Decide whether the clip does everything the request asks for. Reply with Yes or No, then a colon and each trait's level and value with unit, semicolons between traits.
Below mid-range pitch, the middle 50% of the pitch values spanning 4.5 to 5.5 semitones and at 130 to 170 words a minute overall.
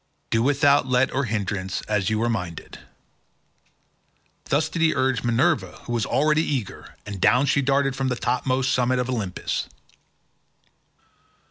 No: low, 130 Hz; average, 3.8 semitones; average, 145 wpm